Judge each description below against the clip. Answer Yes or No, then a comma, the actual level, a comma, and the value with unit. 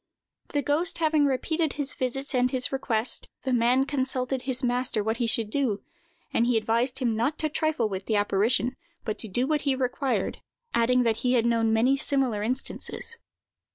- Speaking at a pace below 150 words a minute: No, average, 185 wpm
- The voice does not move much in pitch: No, average, 3.0 semitones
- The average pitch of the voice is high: Yes, very high, 250 Hz